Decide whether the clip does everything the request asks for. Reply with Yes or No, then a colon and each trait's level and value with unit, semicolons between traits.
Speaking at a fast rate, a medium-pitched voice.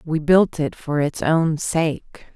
No: average, 180 wpm; medium, 160 Hz